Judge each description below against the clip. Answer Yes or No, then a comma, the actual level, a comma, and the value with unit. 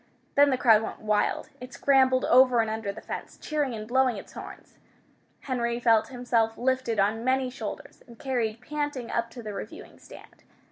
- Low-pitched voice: No, high, 240 Hz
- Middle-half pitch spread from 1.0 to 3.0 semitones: Yes, average, 2.7 semitones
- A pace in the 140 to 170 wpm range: No, average, 180 wpm